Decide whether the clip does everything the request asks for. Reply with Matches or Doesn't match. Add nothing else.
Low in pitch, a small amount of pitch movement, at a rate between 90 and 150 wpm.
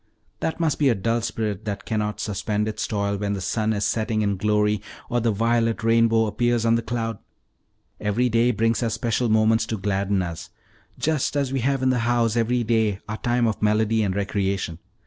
Doesn't match